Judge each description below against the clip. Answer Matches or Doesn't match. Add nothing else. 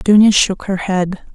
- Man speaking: Doesn't match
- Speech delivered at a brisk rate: Doesn't match